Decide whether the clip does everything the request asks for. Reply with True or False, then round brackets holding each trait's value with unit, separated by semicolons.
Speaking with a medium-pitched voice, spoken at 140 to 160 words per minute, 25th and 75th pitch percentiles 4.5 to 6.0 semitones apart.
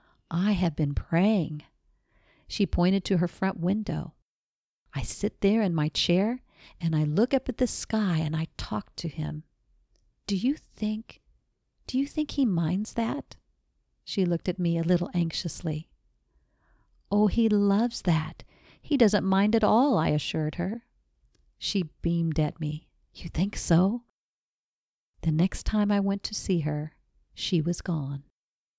True (175 Hz; 155 wpm; 5.1 semitones)